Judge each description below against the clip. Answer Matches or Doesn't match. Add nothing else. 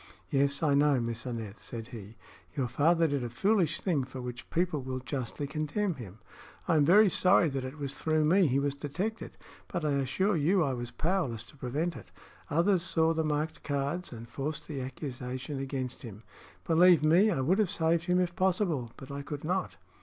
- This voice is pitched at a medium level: Matches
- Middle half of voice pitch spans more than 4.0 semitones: Matches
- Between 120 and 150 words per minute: Doesn't match